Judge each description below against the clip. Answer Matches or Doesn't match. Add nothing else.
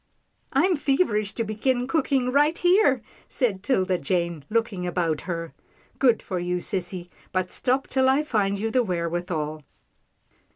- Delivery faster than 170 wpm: Doesn't match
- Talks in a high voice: Matches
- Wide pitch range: Matches